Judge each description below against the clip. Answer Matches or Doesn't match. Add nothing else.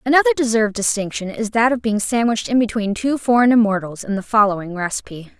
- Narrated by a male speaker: Doesn't match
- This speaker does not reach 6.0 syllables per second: Doesn't match